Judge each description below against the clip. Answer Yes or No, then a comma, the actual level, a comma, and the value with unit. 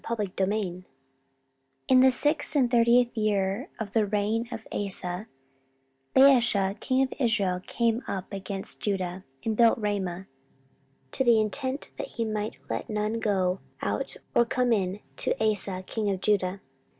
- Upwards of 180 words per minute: No, average, 145 wpm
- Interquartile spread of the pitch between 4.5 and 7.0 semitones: No, average, 3.4 semitones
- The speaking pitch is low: No, high, 215 Hz